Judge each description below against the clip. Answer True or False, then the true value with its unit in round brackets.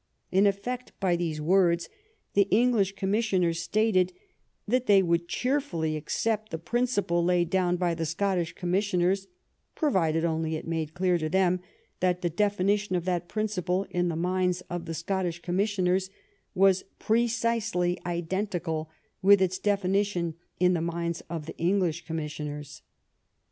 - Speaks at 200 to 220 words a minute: False (150 wpm)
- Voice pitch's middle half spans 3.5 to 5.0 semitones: False (2.9 semitones)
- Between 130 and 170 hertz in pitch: False (180 Hz)